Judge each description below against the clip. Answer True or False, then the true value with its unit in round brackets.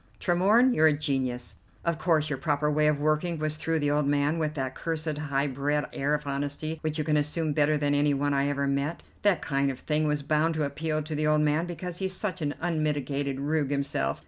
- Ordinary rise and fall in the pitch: False (1.7 semitones)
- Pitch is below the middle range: False (150 Hz)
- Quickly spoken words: True (225 wpm)